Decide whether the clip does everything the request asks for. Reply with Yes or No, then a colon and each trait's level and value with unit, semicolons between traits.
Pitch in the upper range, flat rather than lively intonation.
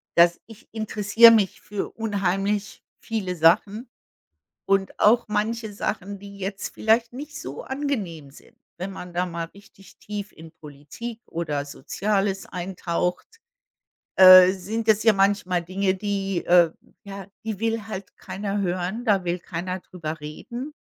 No: high, 195 Hz; average, 3.3 semitones